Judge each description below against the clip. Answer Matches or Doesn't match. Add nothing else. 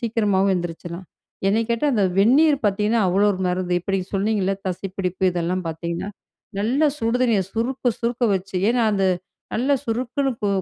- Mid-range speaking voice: Doesn't match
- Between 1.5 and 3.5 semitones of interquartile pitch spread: Doesn't match